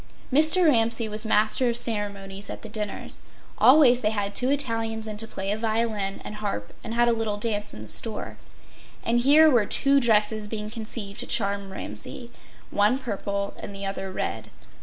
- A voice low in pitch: No, high, 220 Hz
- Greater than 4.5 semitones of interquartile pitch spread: No, average, 2.7 semitones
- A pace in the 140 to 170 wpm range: No, average, 180 wpm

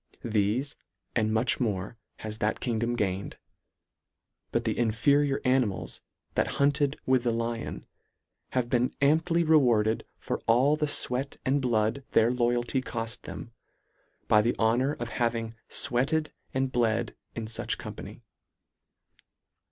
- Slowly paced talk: Yes, slow, 130 wpm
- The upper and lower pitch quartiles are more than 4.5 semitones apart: No, average, 3.1 semitones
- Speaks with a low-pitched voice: Yes, low, 120 Hz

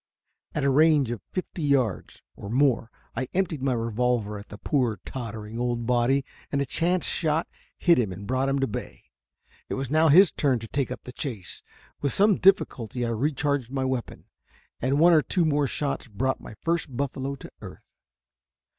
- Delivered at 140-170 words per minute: No, average, 185 wpm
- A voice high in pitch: No, low, 135 Hz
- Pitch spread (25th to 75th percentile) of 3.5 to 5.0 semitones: Yes, average, 3.9 semitones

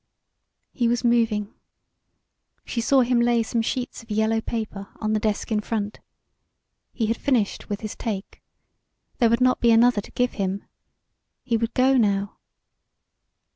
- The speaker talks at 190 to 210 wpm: No, average, 155 wpm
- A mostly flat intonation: Yes, narrow, 2.2 semitones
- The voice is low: No, high, 225 Hz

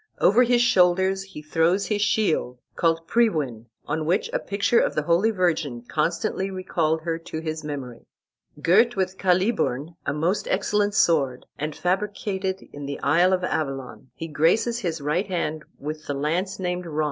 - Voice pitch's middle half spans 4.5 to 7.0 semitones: No, average, 4.1 semitones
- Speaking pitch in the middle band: Yes, medium, 170 Hz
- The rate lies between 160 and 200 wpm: Yes, average, 165 wpm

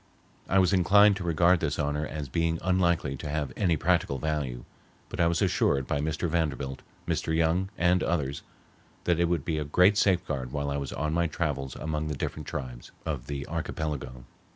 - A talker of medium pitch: No, very low, 80 Hz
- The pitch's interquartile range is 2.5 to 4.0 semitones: Yes, average, 3.4 semitones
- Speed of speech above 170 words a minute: Yes, average, 190 wpm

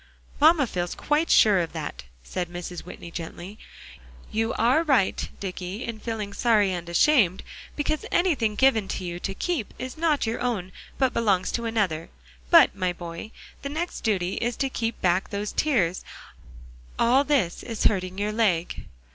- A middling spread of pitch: No, wide, 6.0 semitones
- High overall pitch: Yes, high, 215 Hz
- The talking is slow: No, average, 165 wpm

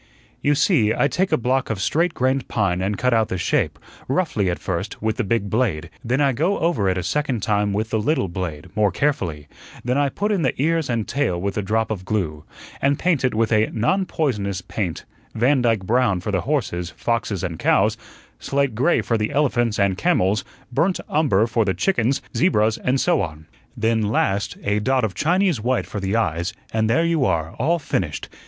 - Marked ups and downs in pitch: Yes, wide, 5.9 semitones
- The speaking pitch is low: Yes, low, 115 Hz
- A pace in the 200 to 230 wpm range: Yes, fast, 205 wpm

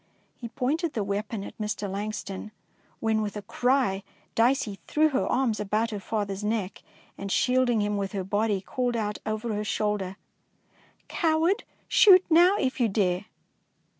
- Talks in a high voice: Yes, high, 215 Hz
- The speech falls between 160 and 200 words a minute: Yes, average, 165 wpm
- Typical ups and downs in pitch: Yes, average, 3.9 semitones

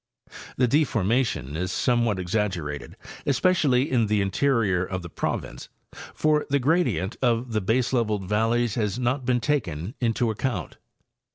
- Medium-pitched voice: No, low, 115 Hz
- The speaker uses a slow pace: Yes, slow, 130 wpm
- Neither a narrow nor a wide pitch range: Yes, average, 4.9 semitones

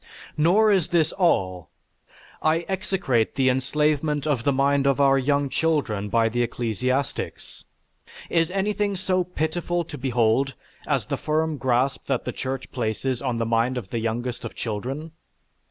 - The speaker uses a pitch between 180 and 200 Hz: No, low, 135 Hz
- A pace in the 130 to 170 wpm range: Yes, average, 155 wpm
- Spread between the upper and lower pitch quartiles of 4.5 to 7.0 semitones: Yes, average, 4.8 semitones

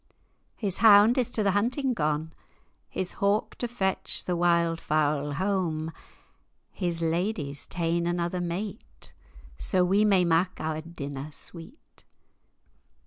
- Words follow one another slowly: Yes, slow, 125 wpm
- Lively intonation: No, average, 3.8 semitones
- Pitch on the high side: No, medium, 175 Hz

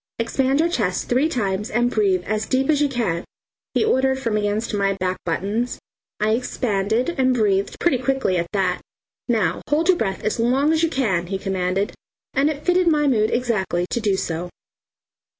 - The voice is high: Yes, high, 225 Hz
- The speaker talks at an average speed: Yes, average, 185 wpm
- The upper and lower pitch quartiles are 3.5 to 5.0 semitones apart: No, wide, 5.5 semitones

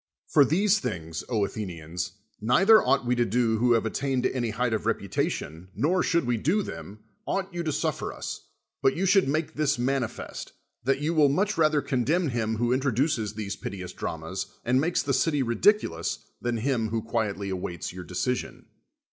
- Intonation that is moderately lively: No, wide, 5.9 semitones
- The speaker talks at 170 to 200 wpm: Yes, average, 180 wpm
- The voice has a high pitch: No, low, 125 Hz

